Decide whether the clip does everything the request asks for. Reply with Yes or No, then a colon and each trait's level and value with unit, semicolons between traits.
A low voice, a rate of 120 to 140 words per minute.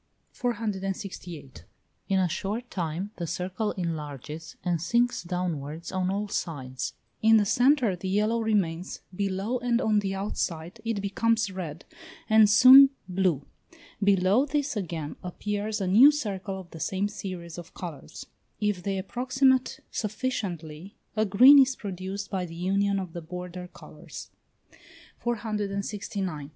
No: high, 195 Hz; slow, 135 wpm